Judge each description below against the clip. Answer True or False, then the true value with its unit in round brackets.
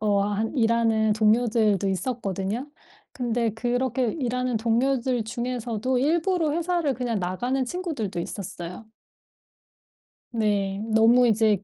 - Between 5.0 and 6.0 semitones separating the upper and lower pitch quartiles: False (3.2 semitones)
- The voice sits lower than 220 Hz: False (230 Hz)